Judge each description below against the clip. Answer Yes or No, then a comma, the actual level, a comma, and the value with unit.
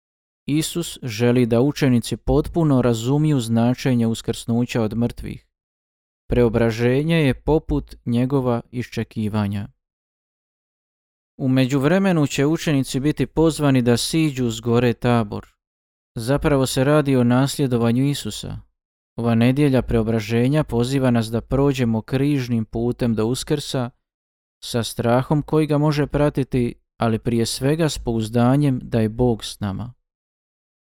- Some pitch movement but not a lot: Yes, average, 3.4 semitones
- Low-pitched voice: Yes, low, 125 Hz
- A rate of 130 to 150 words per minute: No, average, 115 wpm